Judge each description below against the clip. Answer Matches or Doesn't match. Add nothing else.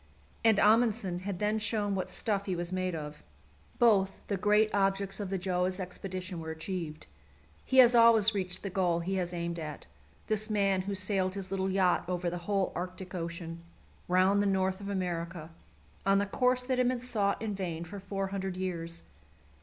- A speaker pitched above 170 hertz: Matches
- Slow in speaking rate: Doesn't match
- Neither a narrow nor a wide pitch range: Doesn't match